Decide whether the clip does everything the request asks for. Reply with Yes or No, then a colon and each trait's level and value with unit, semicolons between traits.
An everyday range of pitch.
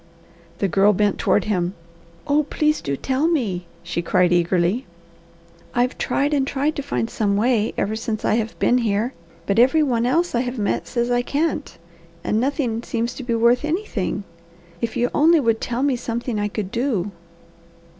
Yes: average, 4.5 semitones